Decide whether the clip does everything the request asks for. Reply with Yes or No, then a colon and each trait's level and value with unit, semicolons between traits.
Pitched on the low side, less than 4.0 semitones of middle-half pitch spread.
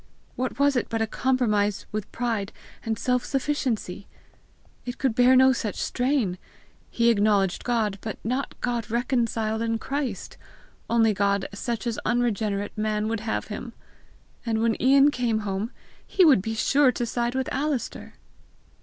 No: high, 230 Hz; average, 2.9 semitones